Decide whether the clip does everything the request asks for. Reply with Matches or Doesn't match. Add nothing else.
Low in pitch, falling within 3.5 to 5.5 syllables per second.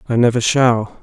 Matches